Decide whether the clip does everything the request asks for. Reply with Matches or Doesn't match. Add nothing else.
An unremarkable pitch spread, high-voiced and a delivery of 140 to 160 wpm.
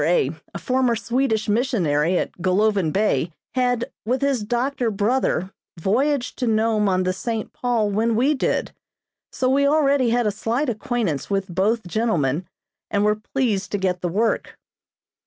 Matches